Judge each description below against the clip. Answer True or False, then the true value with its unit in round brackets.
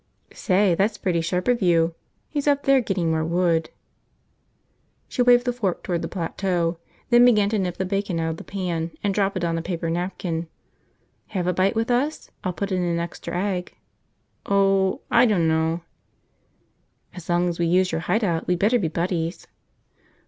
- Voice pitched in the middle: True (180 Hz)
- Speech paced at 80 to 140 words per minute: False (185 wpm)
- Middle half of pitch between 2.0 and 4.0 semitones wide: True (3.2 semitones)